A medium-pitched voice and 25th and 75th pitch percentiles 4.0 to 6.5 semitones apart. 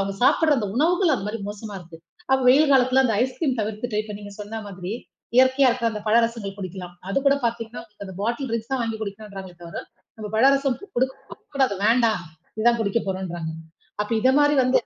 No: high, 225 Hz; average, 4.3 semitones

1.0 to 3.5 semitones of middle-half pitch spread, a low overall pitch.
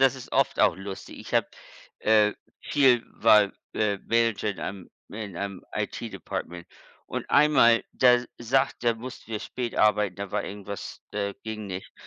Yes: average, 2.9 semitones; low, 105 Hz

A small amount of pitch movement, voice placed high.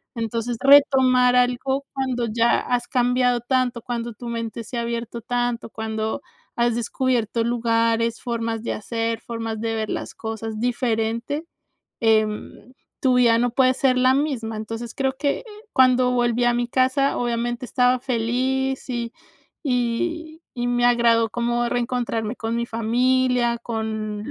Yes: narrow, 1.8 semitones; high, 240 Hz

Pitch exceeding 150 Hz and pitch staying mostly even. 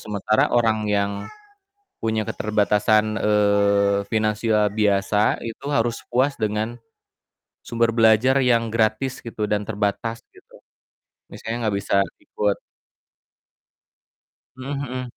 No: low, 110 Hz; narrow, 1.9 semitones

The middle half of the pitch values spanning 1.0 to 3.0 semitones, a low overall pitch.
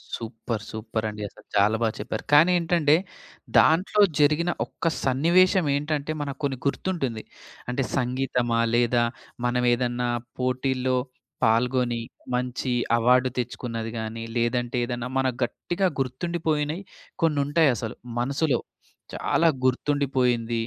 No: average, 3.7 semitones; low, 130 Hz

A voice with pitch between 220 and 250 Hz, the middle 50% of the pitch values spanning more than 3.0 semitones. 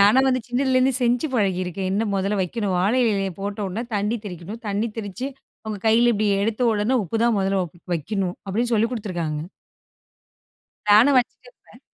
No: high, 210 Hz; average, 3.5 semitones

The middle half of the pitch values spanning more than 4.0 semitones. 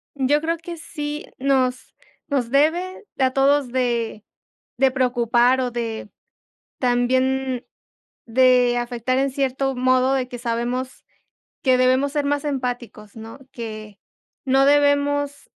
No: narrow, 2.4 semitones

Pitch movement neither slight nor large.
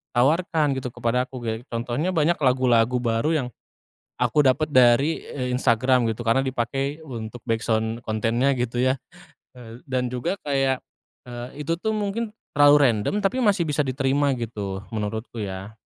Yes: average, 3.8 semitones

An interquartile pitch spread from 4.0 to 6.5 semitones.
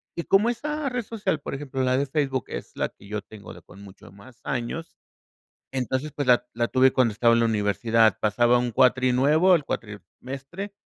Yes: average, 4.8 semitones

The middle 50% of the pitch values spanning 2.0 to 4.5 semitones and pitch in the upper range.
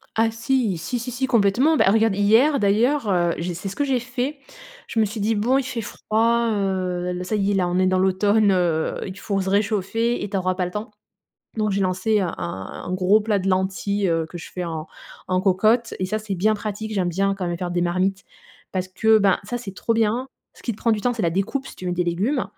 Yes: average, 3.5 semitones; high, 200 Hz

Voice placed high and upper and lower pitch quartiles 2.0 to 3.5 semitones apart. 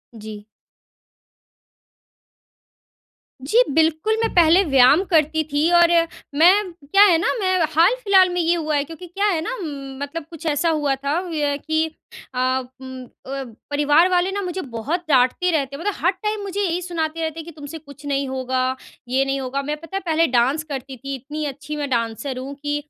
No: very high, 310 Hz; average, 4.1 semitones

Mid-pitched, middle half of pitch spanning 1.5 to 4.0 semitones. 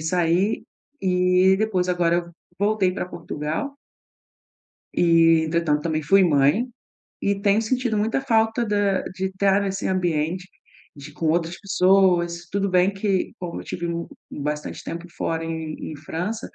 Yes: medium, 180 Hz; average, 3.1 semitones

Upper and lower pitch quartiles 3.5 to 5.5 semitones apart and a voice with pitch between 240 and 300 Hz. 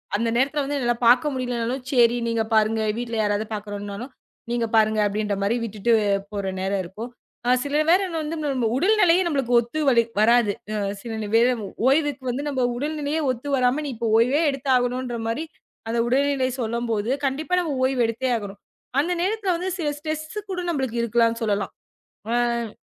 Yes: average, 4.1 semitones; high, 245 Hz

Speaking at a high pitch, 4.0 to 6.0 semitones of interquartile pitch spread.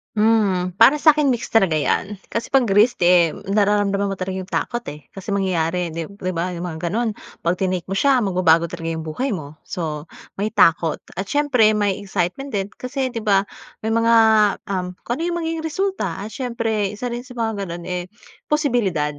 Yes: high, 200 Hz; average, 4.7 semitones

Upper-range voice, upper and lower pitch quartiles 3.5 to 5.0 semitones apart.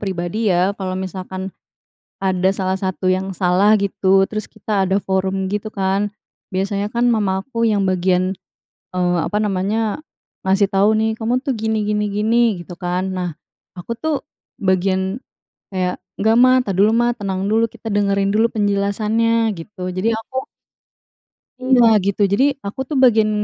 No: high, 200 Hz; average, 2.7 semitones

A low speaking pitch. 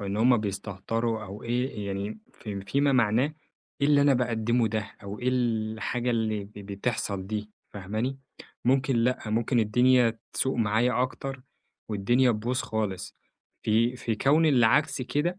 Yes: low, 115 Hz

